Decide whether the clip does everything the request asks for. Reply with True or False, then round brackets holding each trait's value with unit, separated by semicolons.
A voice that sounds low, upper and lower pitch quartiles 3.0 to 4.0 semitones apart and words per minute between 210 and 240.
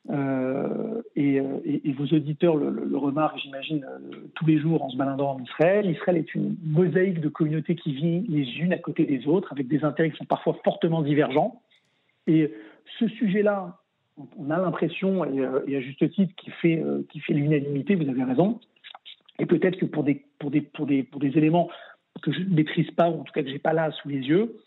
False (155 Hz; 3.6 semitones; 220 wpm)